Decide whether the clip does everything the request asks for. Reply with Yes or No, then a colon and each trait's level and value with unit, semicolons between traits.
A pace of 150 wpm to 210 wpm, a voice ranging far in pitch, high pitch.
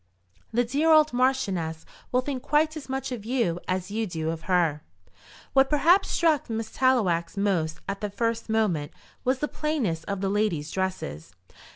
Yes: average, 170 wpm; wide, 7.1 semitones; high, 220 Hz